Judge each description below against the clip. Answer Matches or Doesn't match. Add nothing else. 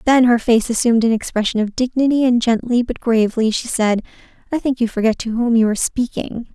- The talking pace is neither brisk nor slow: Doesn't match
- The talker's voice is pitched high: Matches